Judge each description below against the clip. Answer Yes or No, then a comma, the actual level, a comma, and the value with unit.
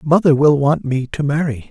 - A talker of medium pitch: Yes, medium, 145 Hz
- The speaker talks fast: Yes, fast, 210 wpm